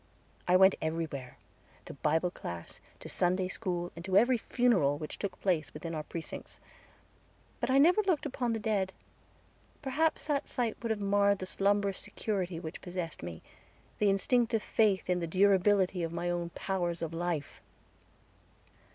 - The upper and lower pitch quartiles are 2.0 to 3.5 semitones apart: No, average, 4.0 semitones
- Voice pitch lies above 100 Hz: Yes, high, 190 Hz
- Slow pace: No, average, 160 wpm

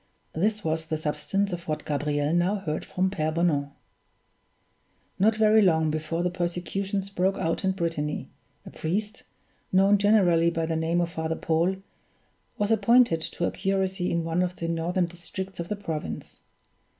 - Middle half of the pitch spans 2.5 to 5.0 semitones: Yes, average, 3.2 semitones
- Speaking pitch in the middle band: Yes, medium, 175 Hz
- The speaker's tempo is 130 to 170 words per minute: Yes, average, 160 wpm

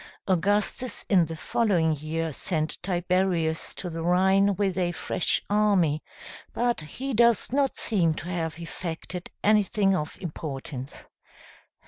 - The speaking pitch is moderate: Yes, medium, 180 Hz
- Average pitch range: Yes, average, 3.9 semitones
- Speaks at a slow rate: Yes, slow, 125 wpm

